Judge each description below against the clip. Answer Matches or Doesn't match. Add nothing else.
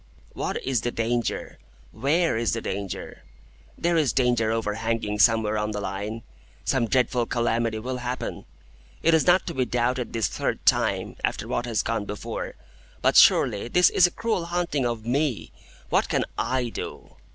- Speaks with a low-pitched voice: Matches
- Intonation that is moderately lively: Matches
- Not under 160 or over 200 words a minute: Matches